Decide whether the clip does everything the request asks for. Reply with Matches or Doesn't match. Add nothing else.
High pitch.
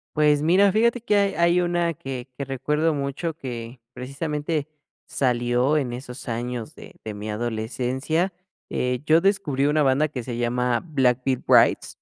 Doesn't match